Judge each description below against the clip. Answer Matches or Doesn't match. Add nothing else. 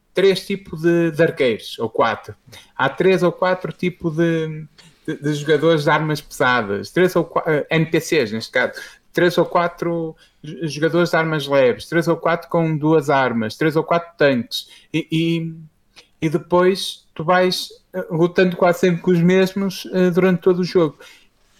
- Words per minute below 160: Doesn't match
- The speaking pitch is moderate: Matches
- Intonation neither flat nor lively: Doesn't match